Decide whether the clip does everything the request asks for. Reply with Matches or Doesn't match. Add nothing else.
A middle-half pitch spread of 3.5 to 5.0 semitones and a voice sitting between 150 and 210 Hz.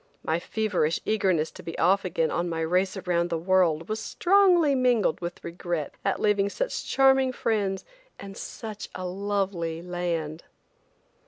Matches